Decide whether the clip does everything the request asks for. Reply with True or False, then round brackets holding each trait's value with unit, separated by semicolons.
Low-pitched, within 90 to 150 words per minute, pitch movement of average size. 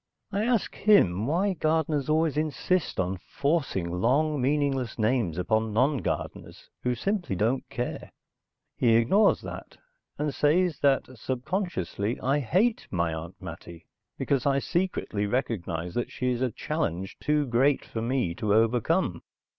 False (130 Hz; 140 wpm; 6.5 semitones)